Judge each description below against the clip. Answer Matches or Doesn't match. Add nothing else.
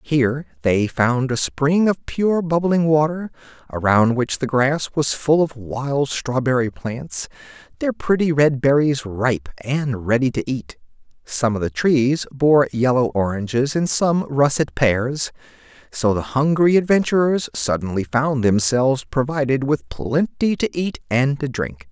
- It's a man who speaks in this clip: Matches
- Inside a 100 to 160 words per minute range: Matches